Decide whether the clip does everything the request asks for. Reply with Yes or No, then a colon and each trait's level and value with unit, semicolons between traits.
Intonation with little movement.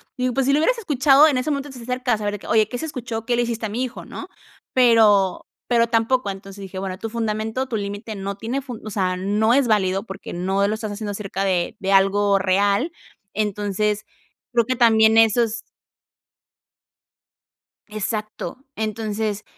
No: average, 3.3 semitones